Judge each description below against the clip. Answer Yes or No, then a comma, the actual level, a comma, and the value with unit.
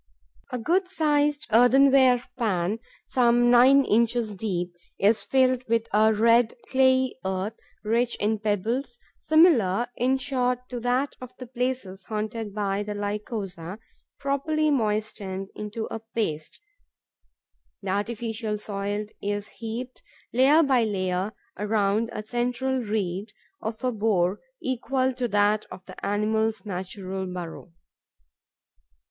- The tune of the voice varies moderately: Yes, average, 3.6 semitones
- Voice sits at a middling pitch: No, high, 225 Hz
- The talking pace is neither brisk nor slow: No, slow, 120 wpm